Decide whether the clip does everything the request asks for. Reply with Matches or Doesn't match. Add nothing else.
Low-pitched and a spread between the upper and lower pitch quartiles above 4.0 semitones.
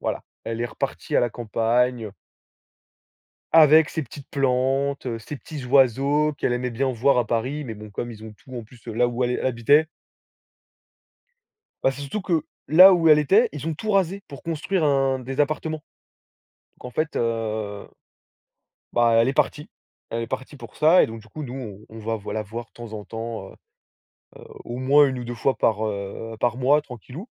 Matches